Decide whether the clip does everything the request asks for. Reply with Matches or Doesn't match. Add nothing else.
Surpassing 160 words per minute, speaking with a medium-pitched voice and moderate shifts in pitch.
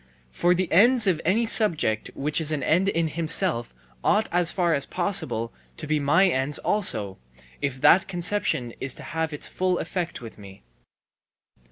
Matches